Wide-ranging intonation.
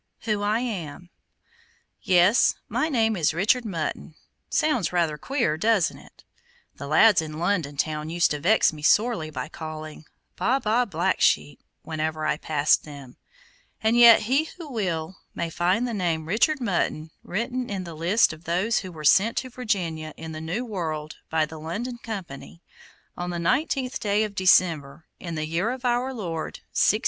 Yes: wide, 6.2 semitones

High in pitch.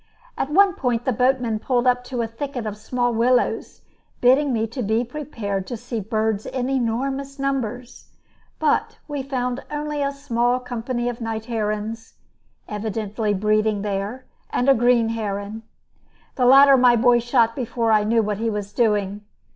Yes: high, 235 Hz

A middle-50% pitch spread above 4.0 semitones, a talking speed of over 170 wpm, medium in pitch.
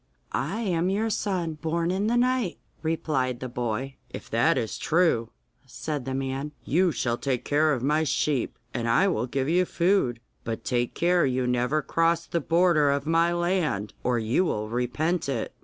Yes: wide, 5.5 semitones; average, 180 wpm; medium, 150 Hz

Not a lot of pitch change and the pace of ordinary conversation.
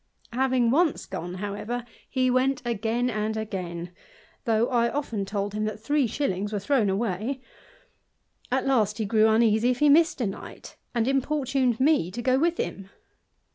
No: average, 3.9 semitones; average, 165 wpm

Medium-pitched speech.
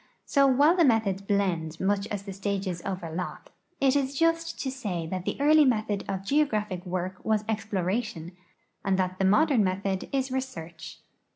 No: high, 200 Hz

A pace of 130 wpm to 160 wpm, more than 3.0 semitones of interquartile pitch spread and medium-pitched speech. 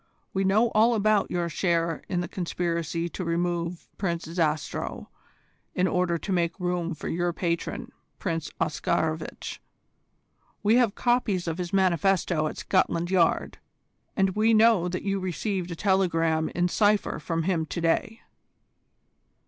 No: average, 140 wpm; narrow, 2.6 semitones; medium, 175 Hz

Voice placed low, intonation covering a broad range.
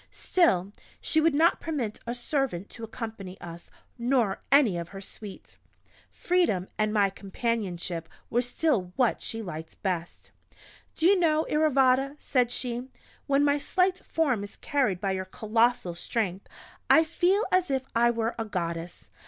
No: high, 235 Hz; wide, 6.8 semitones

